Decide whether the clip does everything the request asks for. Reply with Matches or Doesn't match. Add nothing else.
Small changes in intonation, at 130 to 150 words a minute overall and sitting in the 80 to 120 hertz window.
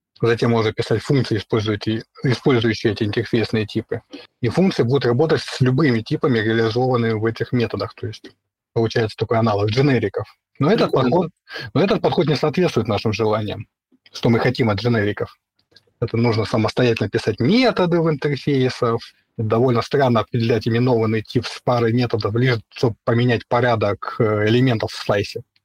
Matches